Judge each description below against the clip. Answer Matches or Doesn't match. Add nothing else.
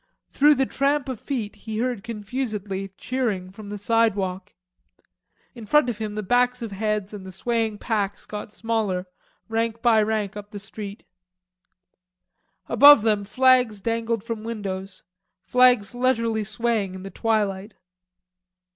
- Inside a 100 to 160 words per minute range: Matches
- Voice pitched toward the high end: Matches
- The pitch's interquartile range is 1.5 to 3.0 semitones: Matches